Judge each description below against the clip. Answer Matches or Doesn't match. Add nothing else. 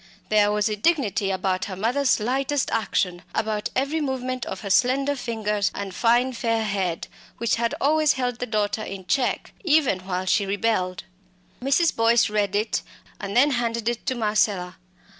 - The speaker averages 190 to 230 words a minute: Doesn't match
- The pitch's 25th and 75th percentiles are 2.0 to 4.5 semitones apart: Matches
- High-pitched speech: Matches